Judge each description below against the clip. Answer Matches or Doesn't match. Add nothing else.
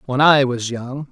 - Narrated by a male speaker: Matches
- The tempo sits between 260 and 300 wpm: Doesn't match